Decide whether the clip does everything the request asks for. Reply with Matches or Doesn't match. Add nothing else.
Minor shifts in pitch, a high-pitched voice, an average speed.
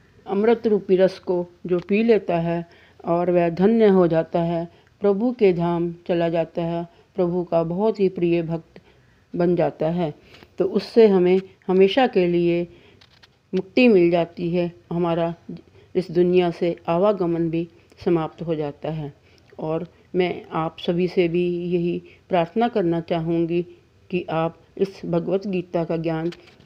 Doesn't match